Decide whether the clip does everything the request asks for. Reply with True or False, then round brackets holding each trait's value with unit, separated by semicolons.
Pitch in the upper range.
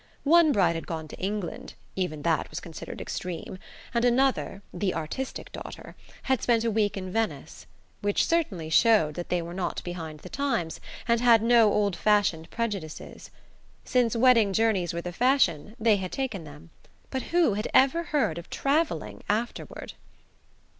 True (205 Hz)